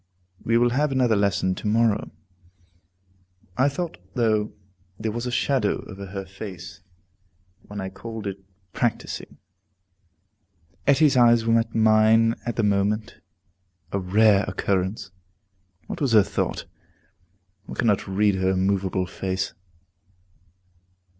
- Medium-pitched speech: No, low, 105 Hz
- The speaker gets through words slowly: Yes, slow, 120 wpm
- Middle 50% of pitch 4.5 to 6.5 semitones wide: No, average, 3.0 semitones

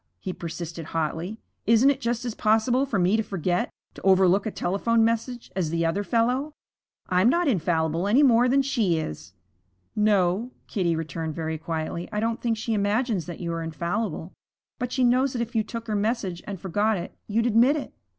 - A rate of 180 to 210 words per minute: Yes, average, 190 wpm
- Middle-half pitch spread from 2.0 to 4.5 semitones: No, wide, 5.4 semitones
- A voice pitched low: No, high, 210 Hz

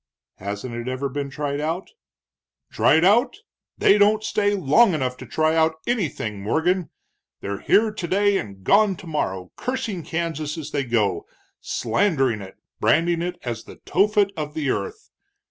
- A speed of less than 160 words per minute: Yes, average, 150 wpm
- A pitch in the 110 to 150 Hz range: No, medium, 160 Hz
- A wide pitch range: Yes, wide, 7.6 semitones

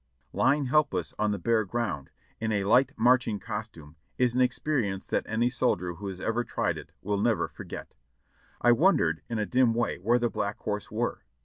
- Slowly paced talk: No, average, 190 wpm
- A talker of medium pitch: No, low, 115 Hz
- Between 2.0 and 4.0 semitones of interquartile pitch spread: Yes, average, 3.7 semitones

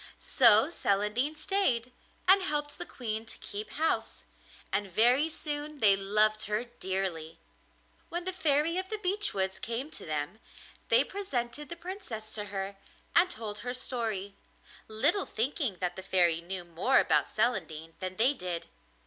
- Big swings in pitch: Yes, wide, 7.4 semitones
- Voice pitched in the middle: No, high, 225 Hz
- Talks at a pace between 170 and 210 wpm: No, average, 155 wpm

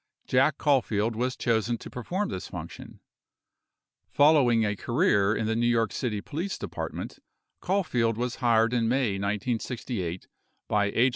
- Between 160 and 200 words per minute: No, average, 140 wpm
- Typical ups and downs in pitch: Yes, average, 3.0 semitones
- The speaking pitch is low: Yes, low, 120 Hz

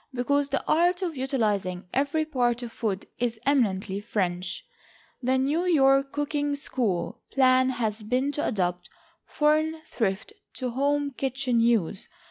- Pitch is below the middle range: No, very high, 255 Hz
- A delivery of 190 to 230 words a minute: No, slow, 135 wpm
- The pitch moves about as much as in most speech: Yes, average, 4.8 semitones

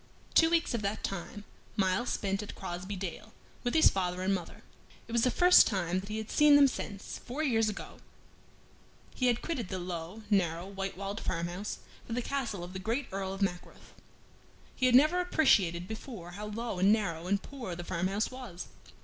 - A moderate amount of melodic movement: Yes, average, 4.6 semitones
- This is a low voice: No, high, 200 Hz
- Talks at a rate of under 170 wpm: No, average, 195 wpm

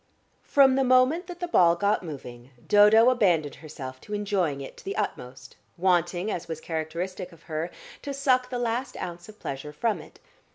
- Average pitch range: No, wide, 7.3 semitones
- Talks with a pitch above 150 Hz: Yes, medium, 185 Hz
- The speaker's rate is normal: Yes, average, 180 wpm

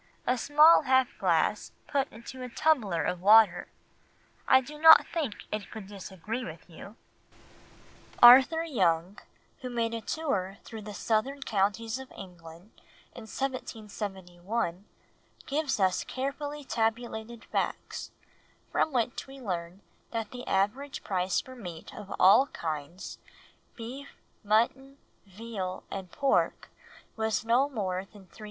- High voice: Yes, high, 225 Hz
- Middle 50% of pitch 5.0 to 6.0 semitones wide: Yes, wide, 5.4 semitones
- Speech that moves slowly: Yes, slow, 130 wpm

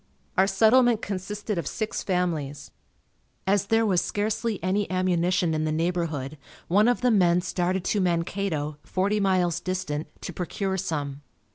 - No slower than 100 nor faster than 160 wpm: Yes, average, 145 wpm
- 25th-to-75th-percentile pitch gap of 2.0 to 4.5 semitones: Yes, average, 3.3 semitones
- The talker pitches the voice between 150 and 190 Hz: Yes, medium, 185 Hz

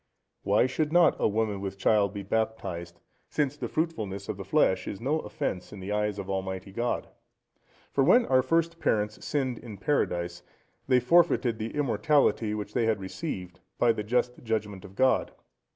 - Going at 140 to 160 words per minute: No, average, 175 wpm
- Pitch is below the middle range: Yes, low, 110 Hz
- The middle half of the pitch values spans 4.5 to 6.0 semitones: Yes, average, 5.2 semitones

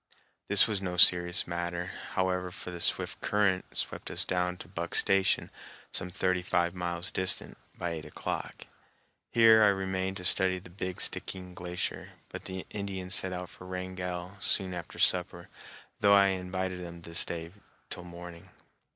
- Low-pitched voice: Yes, very low, 90 Hz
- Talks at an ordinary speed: Yes, average, 160 wpm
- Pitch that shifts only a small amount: Yes, narrow, 1.3 semitones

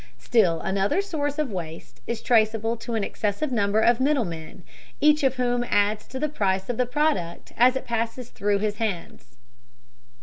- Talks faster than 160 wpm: Yes, average, 170 wpm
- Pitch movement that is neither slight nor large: Yes, average, 4.2 semitones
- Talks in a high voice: Yes, high, 225 Hz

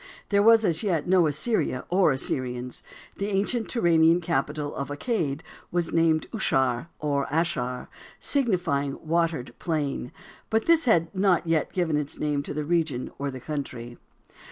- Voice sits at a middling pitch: Yes, medium, 160 Hz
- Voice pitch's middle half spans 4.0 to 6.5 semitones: Yes, average, 4.5 semitones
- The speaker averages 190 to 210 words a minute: No, average, 145 wpm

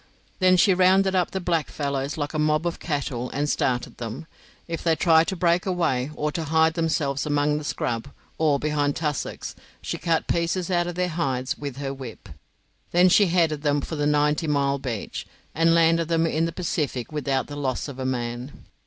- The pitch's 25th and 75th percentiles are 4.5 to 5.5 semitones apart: No, average, 3.2 semitones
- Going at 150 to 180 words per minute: No, average, 195 wpm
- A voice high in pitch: No, medium, 150 Hz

